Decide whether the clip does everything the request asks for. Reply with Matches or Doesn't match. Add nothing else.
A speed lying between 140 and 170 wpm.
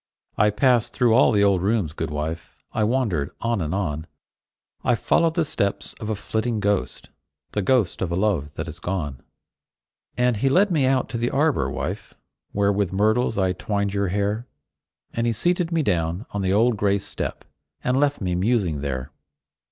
Doesn't match